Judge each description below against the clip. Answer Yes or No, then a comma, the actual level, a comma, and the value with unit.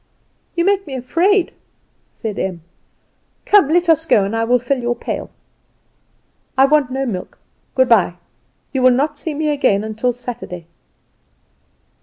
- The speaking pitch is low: No, very high, 255 Hz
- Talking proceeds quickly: No, average, 150 wpm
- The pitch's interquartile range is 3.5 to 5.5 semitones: Yes, average, 5.1 semitones